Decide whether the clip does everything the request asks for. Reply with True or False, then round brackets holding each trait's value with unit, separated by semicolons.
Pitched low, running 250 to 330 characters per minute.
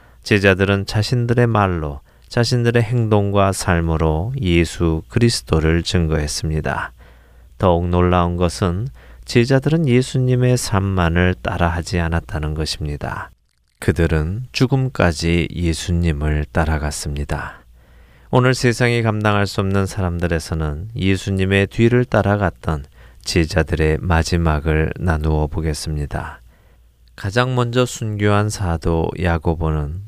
True (85 Hz; 270 characters per minute)